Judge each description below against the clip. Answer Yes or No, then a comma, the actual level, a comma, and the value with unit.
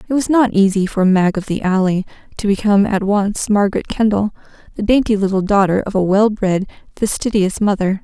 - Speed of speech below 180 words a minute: No, average, 185 wpm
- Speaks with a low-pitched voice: No, high, 200 Hz